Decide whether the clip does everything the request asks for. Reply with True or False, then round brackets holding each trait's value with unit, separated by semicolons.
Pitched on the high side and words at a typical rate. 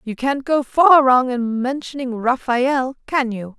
True (255 Hz; 170 wpm)